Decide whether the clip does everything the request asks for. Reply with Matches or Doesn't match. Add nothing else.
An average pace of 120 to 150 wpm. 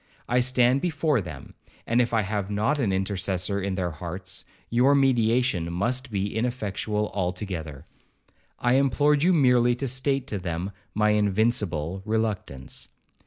Matches